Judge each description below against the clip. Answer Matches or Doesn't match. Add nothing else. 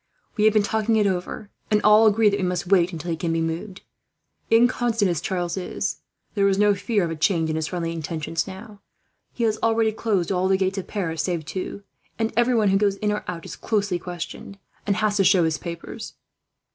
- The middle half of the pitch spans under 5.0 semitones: Matches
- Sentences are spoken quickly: Matches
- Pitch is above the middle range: Matches